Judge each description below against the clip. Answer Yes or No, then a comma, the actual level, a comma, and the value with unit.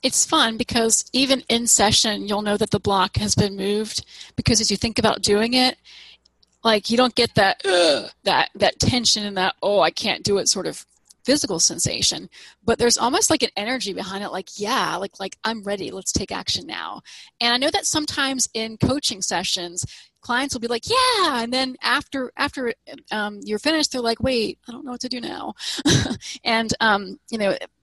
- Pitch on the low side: No, high, 235 Hz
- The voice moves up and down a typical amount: Yes, average, 4.0 semitones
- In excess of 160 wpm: Yes, average, 200 wpm